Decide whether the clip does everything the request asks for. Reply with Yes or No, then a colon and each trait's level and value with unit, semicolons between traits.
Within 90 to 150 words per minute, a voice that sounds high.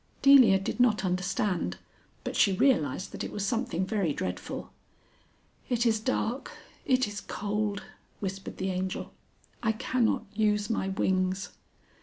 Yes: slow, 135 wpm; high, 205 Hz